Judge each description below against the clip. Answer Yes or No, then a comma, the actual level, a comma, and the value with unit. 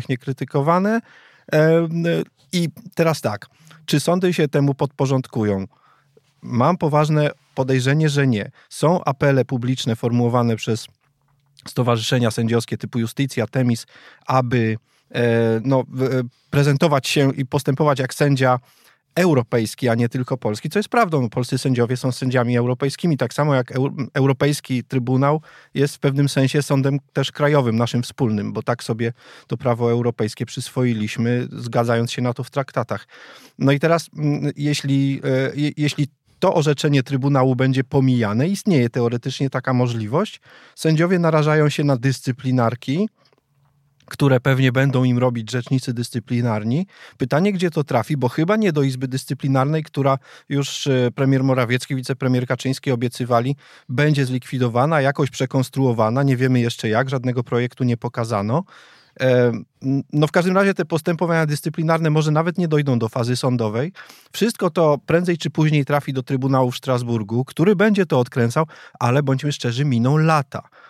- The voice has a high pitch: No, low, 135 Hz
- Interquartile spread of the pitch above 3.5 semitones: No, average, 3.1 semitones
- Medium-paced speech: Yes, average, 135 wpm